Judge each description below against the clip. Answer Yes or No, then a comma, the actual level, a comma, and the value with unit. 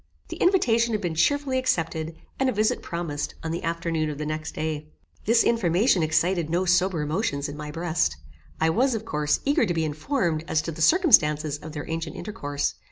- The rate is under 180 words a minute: No, average, 195 wpm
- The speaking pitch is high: No, medium, 165 Hz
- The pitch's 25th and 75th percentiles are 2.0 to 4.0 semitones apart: No, wide, 5.6 semitones